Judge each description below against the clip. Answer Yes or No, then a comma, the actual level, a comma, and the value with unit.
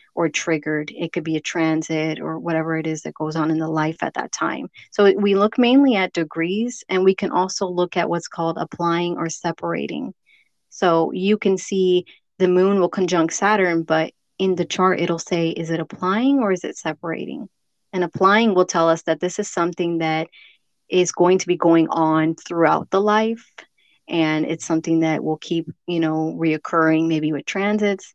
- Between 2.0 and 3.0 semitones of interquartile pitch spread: Yes, narrow, 2.6 semitones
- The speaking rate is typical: Yes, average, 195 wpm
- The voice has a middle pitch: Yes, medium, 170 Hz